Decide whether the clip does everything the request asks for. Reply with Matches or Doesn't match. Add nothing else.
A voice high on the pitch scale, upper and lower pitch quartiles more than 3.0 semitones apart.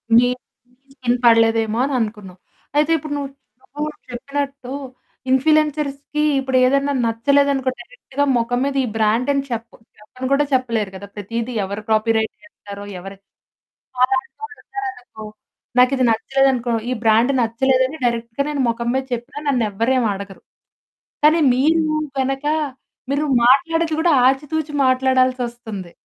Matches